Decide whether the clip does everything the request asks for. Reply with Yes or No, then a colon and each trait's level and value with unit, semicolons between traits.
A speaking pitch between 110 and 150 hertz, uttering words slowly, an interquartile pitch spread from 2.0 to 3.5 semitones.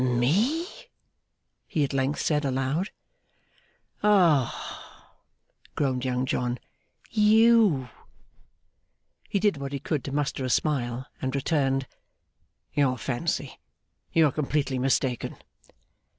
No: medium, 140 Hz; slow, 105 wpm; average, 4.2 semitones